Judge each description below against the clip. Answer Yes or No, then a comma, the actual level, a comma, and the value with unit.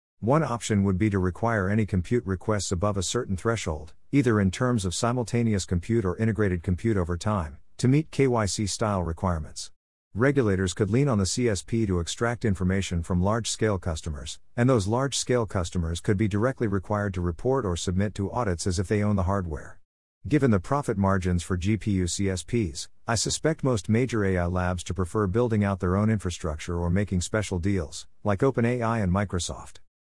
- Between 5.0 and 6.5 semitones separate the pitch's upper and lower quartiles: No, average, 4.1 semitones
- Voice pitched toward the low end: Yes, low, 100 Hz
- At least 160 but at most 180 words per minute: Yes, average, 175 wpm